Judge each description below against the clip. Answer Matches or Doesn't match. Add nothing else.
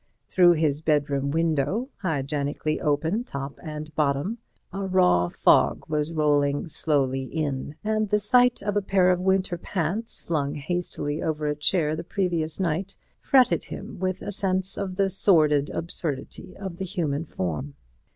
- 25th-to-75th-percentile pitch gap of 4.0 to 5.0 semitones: Matches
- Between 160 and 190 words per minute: Doesn't match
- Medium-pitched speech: Matches